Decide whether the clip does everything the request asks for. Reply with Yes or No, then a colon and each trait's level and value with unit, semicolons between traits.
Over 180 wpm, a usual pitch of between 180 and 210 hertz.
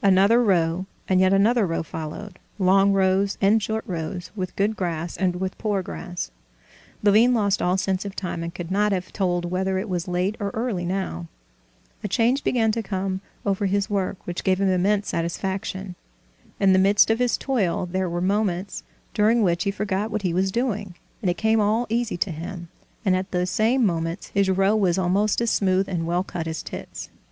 Yes: average, 195 wpm; high, 190 Hz